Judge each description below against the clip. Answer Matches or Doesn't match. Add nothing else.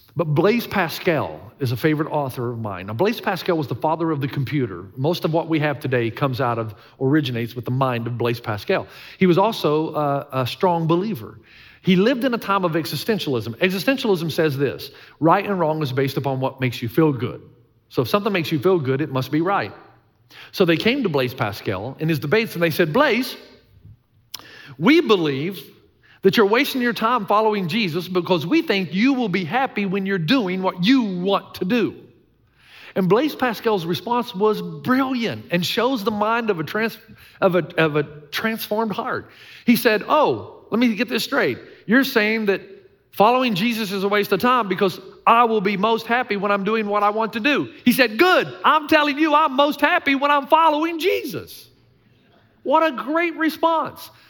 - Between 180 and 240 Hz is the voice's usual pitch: Matches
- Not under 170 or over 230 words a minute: Matches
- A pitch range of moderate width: Doesn't match